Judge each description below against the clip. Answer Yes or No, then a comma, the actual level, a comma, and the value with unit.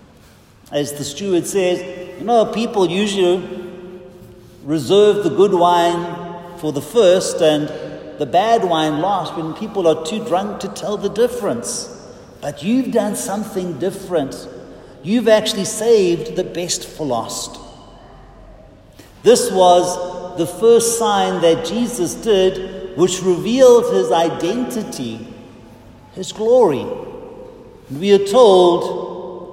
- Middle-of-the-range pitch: Yes, medium, 180 Hz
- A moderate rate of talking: No, slow, 120 wpm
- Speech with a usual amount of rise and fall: Yes, average, 4.0 semitones